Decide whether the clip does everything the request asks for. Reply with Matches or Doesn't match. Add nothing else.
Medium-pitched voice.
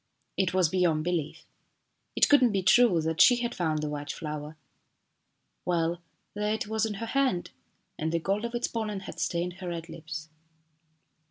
Matches